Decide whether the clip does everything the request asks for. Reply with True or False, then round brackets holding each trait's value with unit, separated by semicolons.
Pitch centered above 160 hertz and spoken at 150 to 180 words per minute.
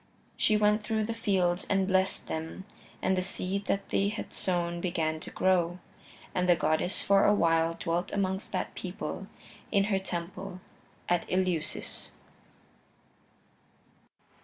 False (185 Hz; 135 wpm)